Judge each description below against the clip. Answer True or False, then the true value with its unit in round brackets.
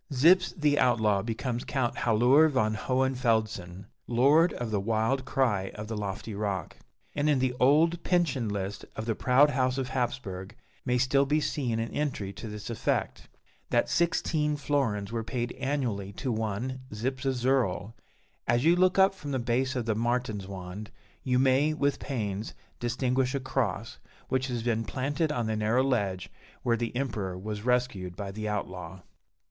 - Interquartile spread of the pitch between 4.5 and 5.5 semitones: False (4.1 semitones)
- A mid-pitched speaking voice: False (120 Hz)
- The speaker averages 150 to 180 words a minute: True (165 wpm)